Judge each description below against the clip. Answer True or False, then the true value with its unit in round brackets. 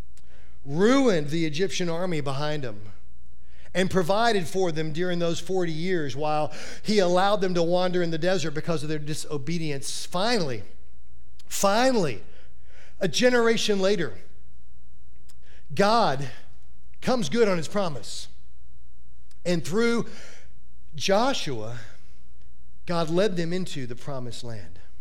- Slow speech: True (115 wpm)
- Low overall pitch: False (150 Hz)